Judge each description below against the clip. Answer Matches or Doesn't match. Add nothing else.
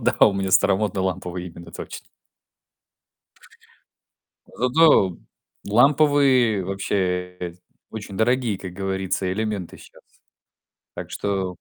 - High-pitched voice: Doesn't match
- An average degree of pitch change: Matches